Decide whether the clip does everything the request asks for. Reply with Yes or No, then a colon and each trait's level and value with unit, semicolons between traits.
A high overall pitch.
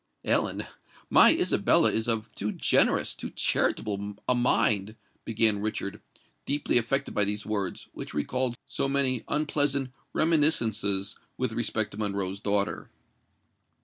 No: low, 110 Hz